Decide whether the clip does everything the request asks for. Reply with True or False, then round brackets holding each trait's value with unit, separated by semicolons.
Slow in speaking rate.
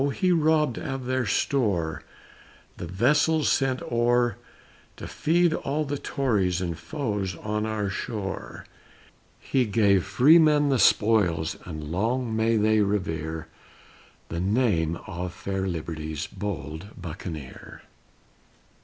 True (115 wpm)